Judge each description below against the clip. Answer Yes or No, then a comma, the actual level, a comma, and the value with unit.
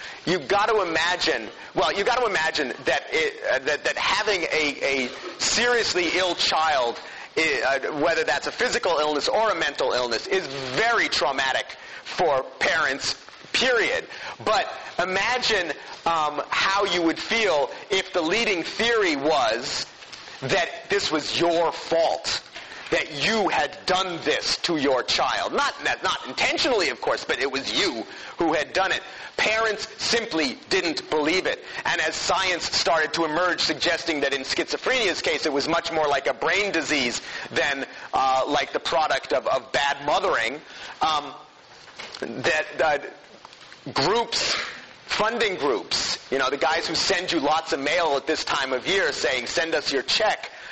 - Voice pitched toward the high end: Yes, high, 220 Hz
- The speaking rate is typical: Yes, average, 155 wpm